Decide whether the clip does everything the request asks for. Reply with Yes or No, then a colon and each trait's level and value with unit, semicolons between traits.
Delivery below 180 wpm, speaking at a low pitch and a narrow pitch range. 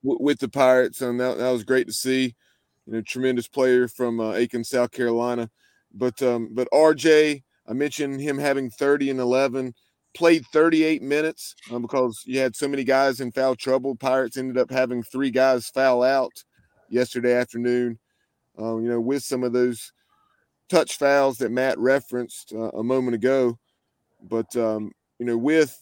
Yes: average, 170 wpm; low, 130 Hz; narrow, 2.1 semitones